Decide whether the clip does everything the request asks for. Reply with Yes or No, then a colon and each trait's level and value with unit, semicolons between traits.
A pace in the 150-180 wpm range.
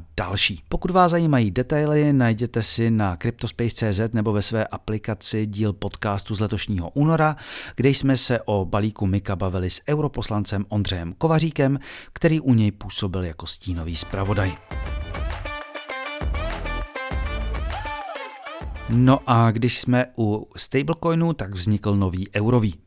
No: average, 120 wpm